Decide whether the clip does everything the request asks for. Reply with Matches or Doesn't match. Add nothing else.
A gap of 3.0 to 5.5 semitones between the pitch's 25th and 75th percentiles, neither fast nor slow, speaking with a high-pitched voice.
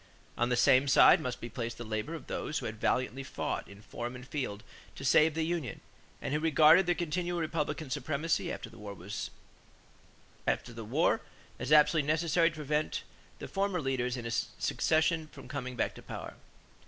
Doesn't match